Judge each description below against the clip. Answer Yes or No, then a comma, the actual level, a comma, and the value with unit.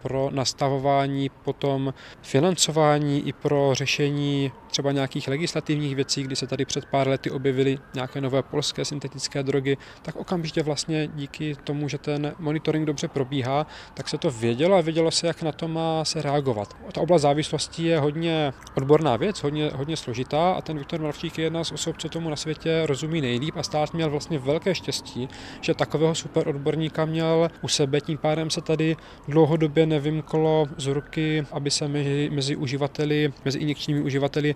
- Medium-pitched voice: Yes, medium, 150 Hz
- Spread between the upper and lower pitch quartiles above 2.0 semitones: Yes, narrow, 2.4 semitones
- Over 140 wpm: Yes, fast, 170 wpm